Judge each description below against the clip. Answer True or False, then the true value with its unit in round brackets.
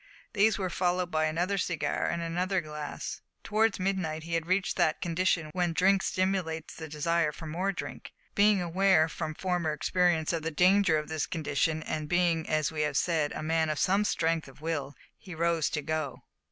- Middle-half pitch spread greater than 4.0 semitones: False (2.8 semitones)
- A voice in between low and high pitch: True (165 Hz)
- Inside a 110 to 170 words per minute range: False (190 wpm)